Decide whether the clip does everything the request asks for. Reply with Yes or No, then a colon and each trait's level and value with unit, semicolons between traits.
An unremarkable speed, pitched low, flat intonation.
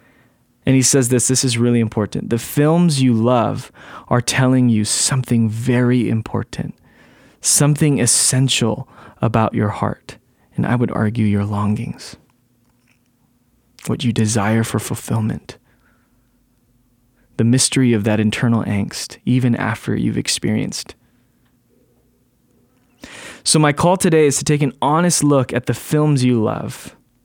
No: slow, 130 wpm; low, 125 Hz; narrow, 2.3 semitones